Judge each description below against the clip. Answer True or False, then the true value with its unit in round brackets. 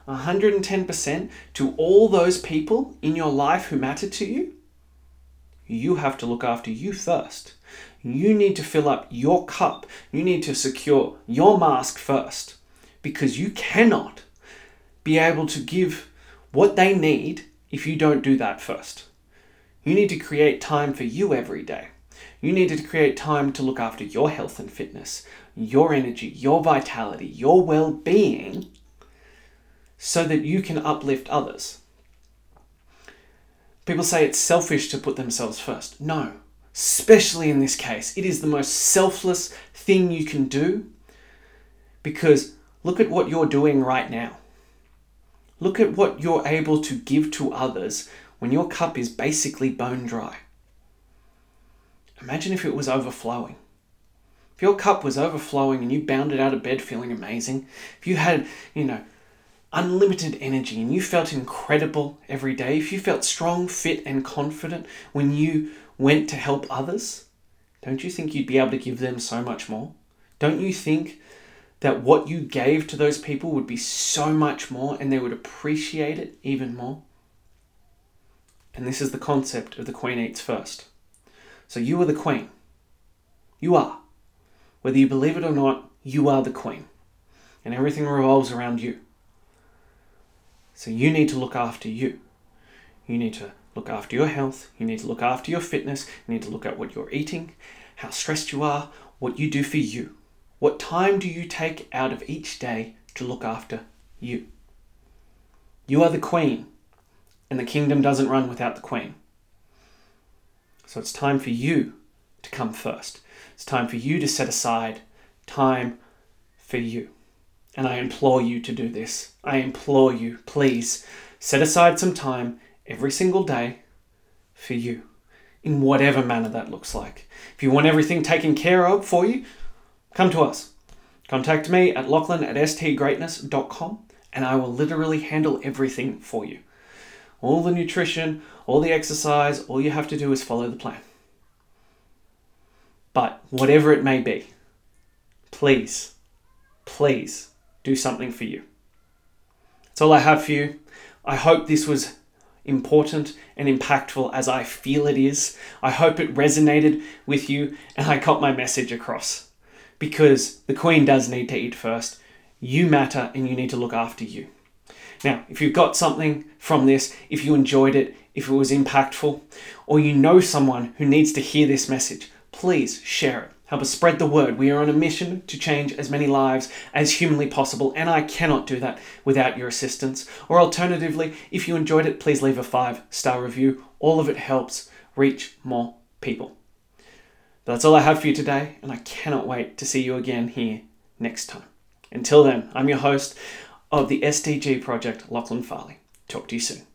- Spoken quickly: False (170 wpm)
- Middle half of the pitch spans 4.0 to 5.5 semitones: False (3.6 semitones)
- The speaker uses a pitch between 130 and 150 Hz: True (140 Hz)